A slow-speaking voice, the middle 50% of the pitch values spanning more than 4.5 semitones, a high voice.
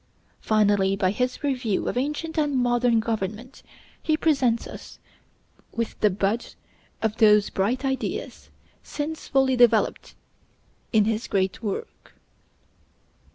No: slow, 115 wpm; average, 4.0 semitones; high, 230 Hz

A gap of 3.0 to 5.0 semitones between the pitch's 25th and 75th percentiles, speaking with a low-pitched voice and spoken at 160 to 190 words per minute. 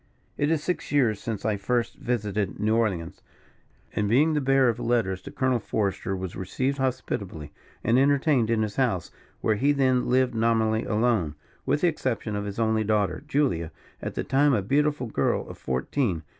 Yes: average, 4.5 semitones; low, 115 Hz; average, 180 wpm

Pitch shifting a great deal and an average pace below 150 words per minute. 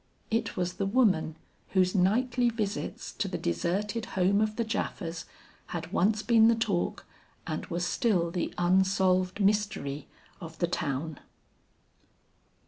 No: average, 3.8 semitones; slow, 135 wpm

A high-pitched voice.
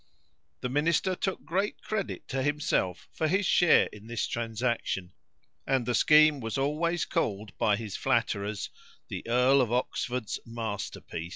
No: low, 125 Hz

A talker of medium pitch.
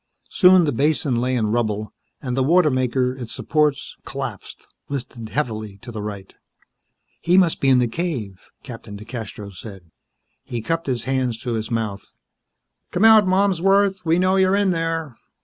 No: low, 130 Hz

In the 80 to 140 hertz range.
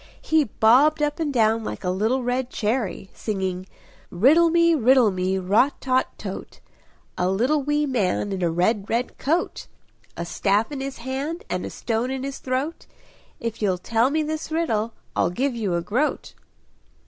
No: high, 245 Hz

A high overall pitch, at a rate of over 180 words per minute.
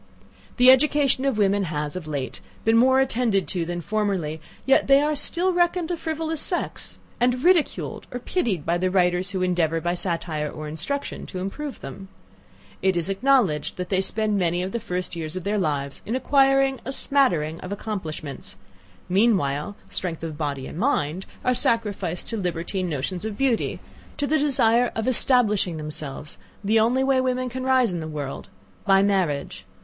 No: high, 195 Hz; average, 175 wpm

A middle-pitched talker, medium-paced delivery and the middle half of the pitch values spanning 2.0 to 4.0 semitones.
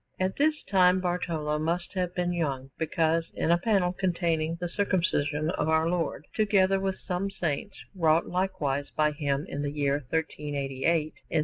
Yes: medium, 170 Hz; average, 170 wpm; average, 3.6 semitones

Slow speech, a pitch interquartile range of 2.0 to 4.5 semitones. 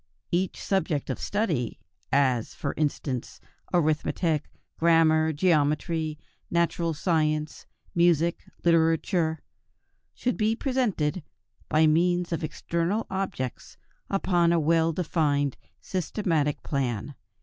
Yes: slow, 95 wpm; narrow, 2.6 semitones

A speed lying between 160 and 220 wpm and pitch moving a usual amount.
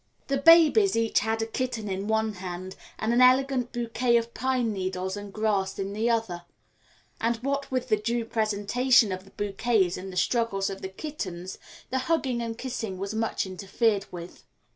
Yes: average, 180 wpm; average, 4.1 semitones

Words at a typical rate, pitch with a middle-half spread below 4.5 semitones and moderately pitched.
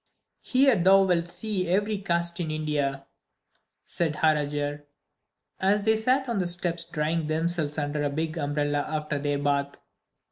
Yes: average, 145 wpm; average, 3.9 semitones; medium, 160 Hz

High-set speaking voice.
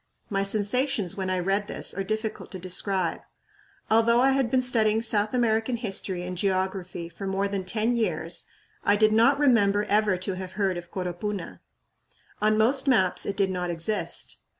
Yes: high, 205 Hz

